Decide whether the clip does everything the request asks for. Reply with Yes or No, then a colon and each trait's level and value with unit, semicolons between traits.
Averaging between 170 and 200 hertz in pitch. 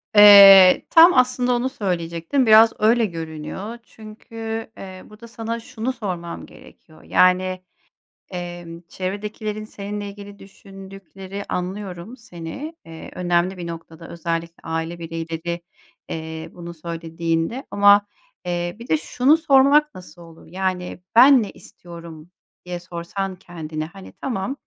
Yes: medium, 185 Hz